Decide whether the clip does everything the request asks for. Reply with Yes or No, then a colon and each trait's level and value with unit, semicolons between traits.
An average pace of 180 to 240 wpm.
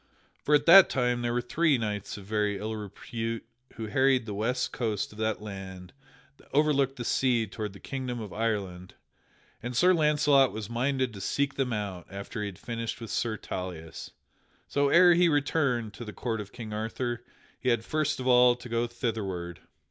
Yes: average, 190 wpm